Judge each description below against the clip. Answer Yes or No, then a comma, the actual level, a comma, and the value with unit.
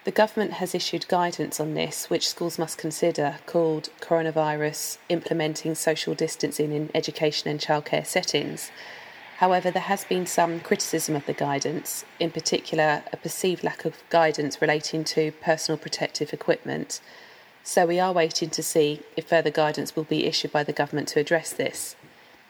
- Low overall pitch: No, medium, 160 Hz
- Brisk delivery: No, average, 160 wpm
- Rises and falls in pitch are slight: Yes, narrow, 1.9 semitones